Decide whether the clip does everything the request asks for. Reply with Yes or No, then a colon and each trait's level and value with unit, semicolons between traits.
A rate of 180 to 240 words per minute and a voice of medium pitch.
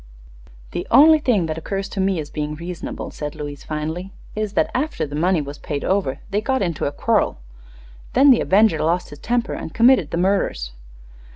Yes: average, 190 wpm; medium, 180 Hz